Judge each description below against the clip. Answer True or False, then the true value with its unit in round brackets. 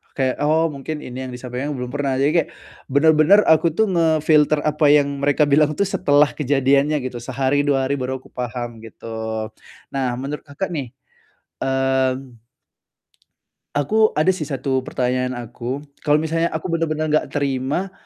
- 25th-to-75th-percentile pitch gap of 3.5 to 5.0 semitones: False (2.9 semitones)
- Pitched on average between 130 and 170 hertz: True (140 Hz)